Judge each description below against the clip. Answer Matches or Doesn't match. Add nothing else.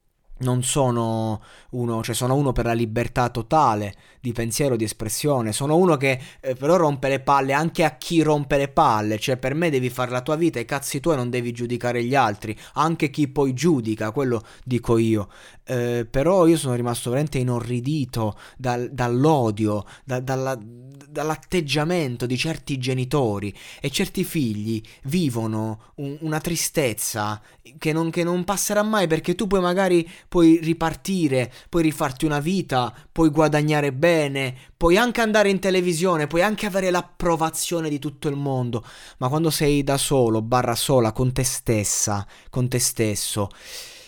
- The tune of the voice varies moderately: Matches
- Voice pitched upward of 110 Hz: Matches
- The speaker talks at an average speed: Matches